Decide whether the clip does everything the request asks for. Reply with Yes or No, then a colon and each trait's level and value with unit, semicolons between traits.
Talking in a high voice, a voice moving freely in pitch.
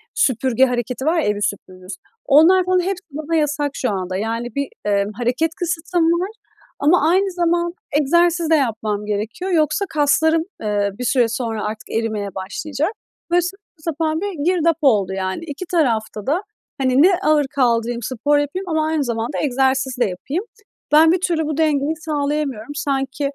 Yes: very high, 290 Hz; wide, 6.1 semitones